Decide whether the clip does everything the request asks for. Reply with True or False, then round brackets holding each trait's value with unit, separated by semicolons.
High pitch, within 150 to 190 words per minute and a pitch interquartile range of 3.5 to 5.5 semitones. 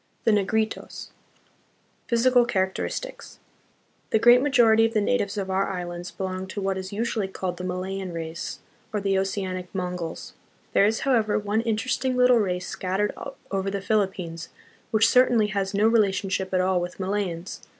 False (195 Hz; 155 wpm; 3.0 semitones)